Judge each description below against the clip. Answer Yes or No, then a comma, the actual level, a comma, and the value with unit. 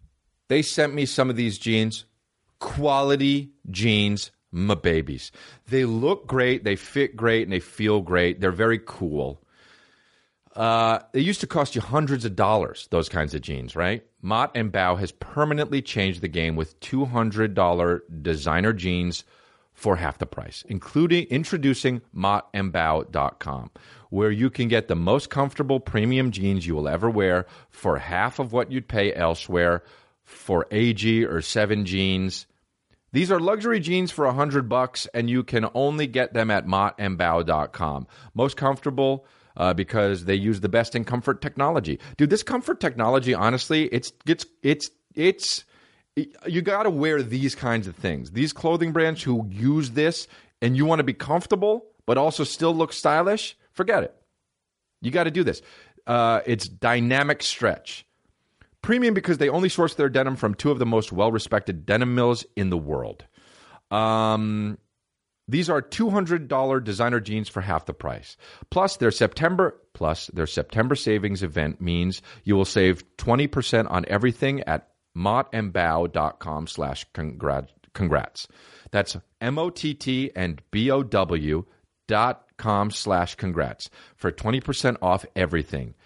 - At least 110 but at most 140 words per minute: No, average, 155 wpm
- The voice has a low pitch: Yes, low, 115 Hz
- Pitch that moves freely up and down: Yes, wide, 6.5 semitones